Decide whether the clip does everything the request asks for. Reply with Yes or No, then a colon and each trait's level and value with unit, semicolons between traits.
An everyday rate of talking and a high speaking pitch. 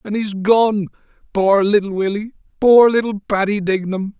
Yes: average, 145 wpm; high, 205 Hz